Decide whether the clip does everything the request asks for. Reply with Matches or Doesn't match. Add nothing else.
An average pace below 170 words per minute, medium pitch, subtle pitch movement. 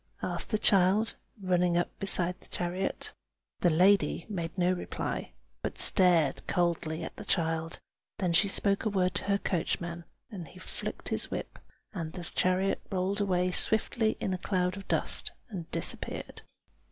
Matches